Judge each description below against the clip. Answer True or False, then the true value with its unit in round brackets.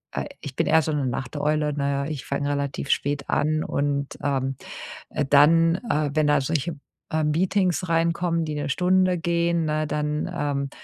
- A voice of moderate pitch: True (150 Hz)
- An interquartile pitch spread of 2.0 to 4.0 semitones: True (2.7 semitones)